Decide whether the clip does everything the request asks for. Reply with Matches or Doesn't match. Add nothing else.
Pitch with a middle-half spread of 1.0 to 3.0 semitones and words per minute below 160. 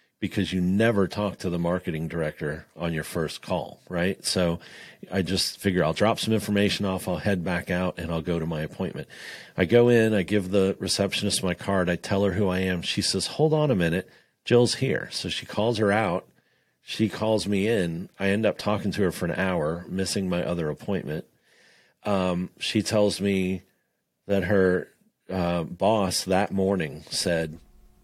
Doesn't match